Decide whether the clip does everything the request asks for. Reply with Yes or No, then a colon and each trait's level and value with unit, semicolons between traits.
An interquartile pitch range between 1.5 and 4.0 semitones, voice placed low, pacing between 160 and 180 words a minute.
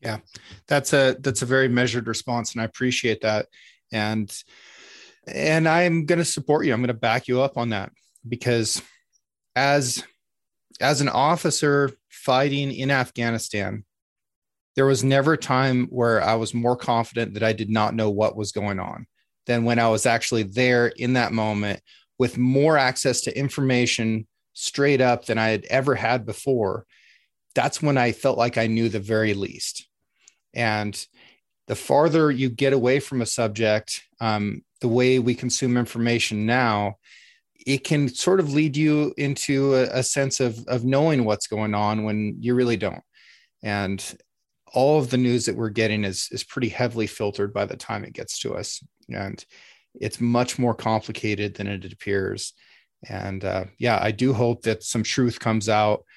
Yes: average, 3.3 semitones; low, 120 Hz; average, 170 wpm